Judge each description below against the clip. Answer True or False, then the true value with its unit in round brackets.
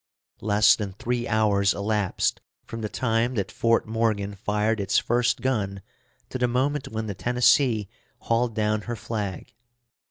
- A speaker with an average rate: True (150 wpm)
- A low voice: True (110 Hz)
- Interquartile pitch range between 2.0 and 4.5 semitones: True (2.5 semitones)